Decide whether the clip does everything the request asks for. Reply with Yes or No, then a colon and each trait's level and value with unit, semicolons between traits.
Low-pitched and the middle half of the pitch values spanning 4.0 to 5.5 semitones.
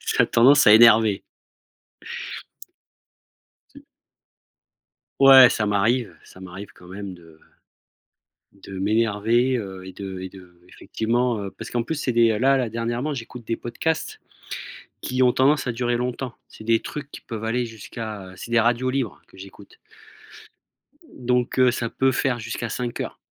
No: low, 115 Hz; average, 3.6 semitones